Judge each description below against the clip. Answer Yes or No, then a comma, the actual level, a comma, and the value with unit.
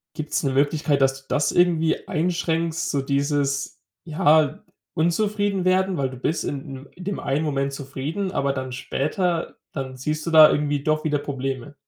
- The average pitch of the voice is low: No, medium, 150 Hz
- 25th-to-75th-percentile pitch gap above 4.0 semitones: No, average, 3.3 semitones